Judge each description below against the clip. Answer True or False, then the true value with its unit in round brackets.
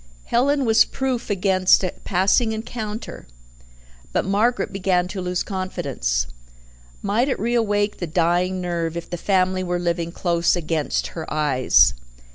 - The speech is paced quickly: False (135 wpm)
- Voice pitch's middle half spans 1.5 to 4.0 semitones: True (3.6 semitones)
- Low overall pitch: False (185 Hz)